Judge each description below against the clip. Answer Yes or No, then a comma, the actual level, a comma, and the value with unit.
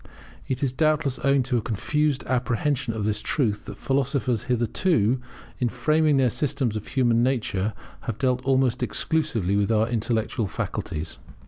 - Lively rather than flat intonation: No, average, 3.7 semitones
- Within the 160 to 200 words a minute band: No, average, 150 wpm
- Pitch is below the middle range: Yes, low, 125 Hz